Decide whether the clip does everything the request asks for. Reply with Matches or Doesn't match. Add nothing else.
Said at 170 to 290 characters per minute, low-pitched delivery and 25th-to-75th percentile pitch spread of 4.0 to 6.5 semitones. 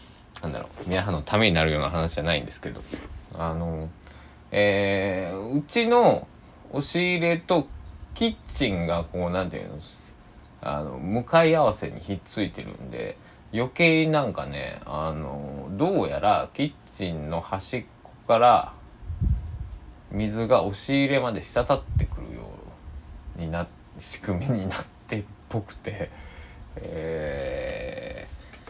Doesn't match